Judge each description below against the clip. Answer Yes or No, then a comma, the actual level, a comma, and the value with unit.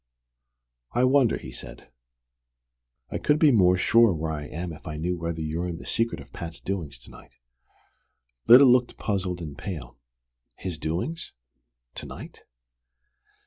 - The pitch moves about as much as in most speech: No, wide, 6.6 semitones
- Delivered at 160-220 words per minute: No, average, 150 wpm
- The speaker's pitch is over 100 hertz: No, very low, 90 Hz